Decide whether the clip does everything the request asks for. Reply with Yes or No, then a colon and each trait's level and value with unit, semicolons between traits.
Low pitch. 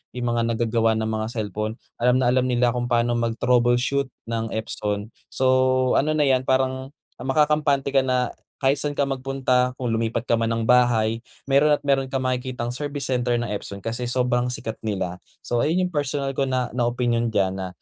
Yes: low, 125 Hz